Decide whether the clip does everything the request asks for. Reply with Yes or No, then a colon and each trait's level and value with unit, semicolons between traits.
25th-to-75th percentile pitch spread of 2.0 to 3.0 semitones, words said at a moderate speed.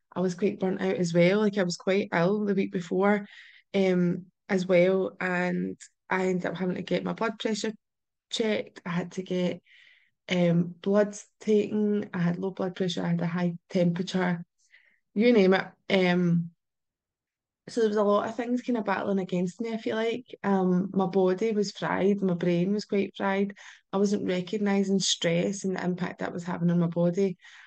Yes: narrow, 2.5 semitones; average, 190 wpm